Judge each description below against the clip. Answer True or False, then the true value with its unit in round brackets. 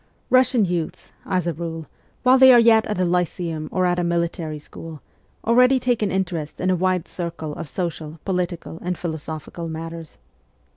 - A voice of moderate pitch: True (175 Hz)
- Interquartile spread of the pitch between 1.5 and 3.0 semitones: True (2.7 semitones)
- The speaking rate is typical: True (175 wpm)